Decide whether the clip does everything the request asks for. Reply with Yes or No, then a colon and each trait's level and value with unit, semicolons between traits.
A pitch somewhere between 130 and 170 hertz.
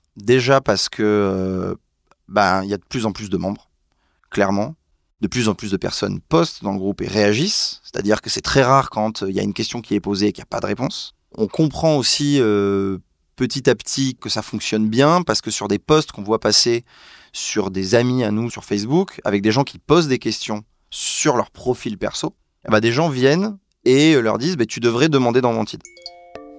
No: low, 110 Hz